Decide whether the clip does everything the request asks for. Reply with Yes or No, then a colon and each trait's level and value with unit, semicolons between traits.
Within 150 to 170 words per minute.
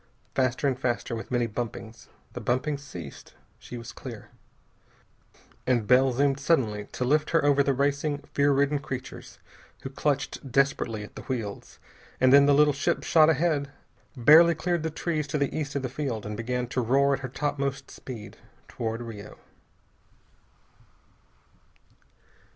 Yes: average, 155 wpm